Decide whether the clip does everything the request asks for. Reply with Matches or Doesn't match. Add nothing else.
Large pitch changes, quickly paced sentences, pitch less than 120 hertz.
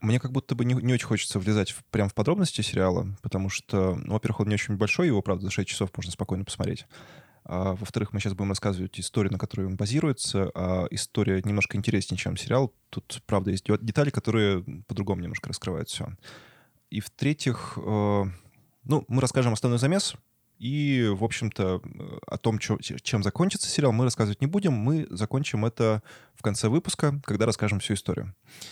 Doesn't match